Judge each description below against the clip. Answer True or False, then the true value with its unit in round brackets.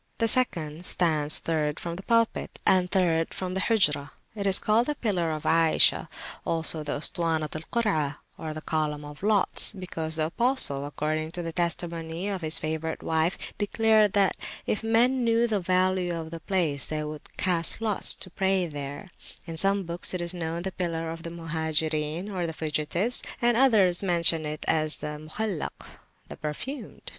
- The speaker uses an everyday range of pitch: True (3.9 semitones)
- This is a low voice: False (170 Hz)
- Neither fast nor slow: True (175 wpm)